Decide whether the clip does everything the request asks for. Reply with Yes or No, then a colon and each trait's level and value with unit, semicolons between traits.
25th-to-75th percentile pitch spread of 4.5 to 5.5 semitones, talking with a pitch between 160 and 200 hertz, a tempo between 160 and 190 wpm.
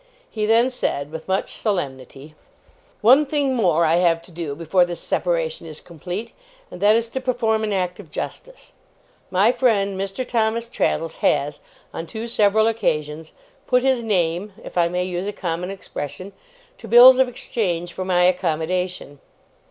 Yes: average, 5.2 semitones; medium, 185 Hz; average, 165 wpm